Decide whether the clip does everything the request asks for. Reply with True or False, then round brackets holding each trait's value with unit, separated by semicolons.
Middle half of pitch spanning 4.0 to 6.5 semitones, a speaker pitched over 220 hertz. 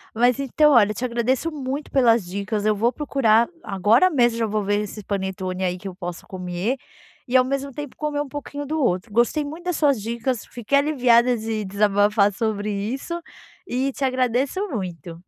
True (5.1 semitones; 235 Hz)